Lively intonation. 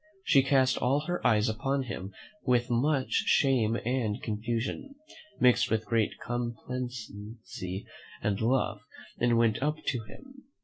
No: average, 3.3 semitones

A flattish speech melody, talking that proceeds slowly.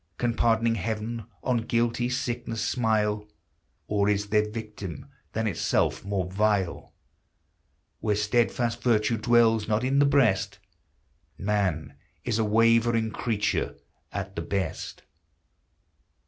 Yes: narrow, 2.3 semitones; slow, 115 wpm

